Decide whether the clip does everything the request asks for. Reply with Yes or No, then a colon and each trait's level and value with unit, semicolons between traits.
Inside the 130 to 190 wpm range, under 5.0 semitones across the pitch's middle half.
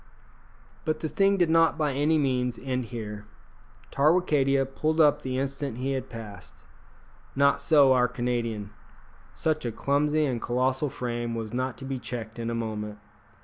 Yes: average, 160 wpm; average, 3.9 semitones